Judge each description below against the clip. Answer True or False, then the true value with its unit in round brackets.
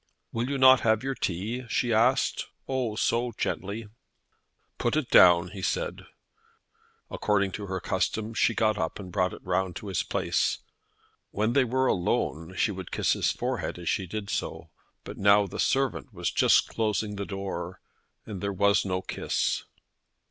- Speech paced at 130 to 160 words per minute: False (170 wpm)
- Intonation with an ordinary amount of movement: True (3.8 semitones)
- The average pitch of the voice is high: False (105 Hz)